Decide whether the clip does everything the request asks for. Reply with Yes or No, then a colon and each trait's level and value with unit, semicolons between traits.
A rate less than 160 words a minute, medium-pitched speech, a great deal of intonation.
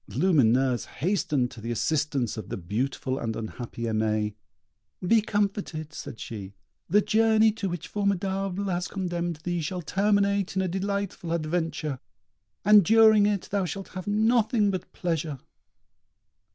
Yes: average, 140 wpm; medium, 180 Hz; wide, 6.7 semitones